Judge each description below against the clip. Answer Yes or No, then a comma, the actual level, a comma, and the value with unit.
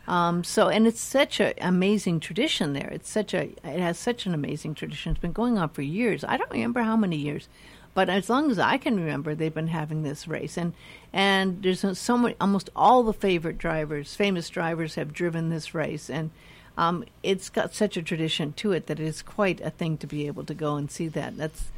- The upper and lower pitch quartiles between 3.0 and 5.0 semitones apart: Yes, average, 4.0 semitones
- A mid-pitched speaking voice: Yes, medium, 170 Hz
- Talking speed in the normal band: No, fast, 250 wpm